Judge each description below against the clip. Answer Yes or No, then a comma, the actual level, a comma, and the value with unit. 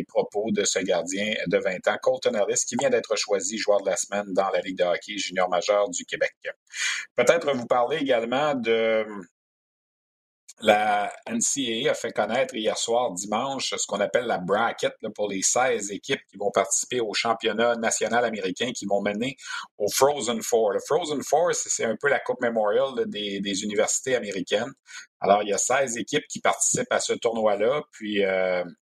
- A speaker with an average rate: Yes, average, 180 wpm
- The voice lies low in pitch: Yes, low, 120 Hz